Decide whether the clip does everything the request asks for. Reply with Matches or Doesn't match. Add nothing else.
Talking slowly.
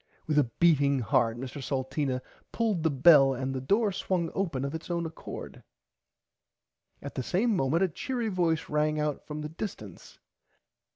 Doesn't match